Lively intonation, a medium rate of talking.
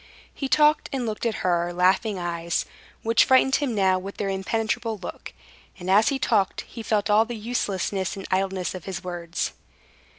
No: average, 3.6 semitones; average, 175 wpm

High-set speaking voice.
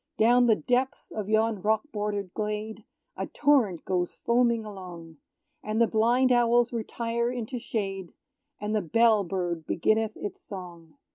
Yes: high, 215 Hz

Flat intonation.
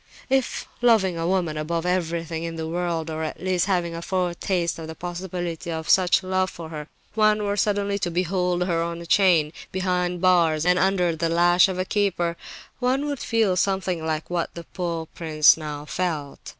Yes: narrow, 2.2 semitones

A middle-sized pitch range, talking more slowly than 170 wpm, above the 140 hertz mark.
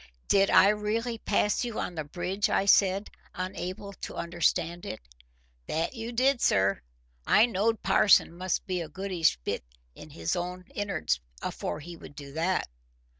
Yes: average, 3.8 semitones; average, 160 wpm; medium, 185 Hz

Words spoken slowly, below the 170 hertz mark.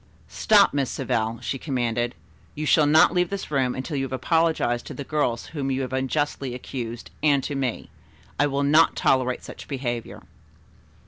No: average, 175 wpm; low, 135 Hz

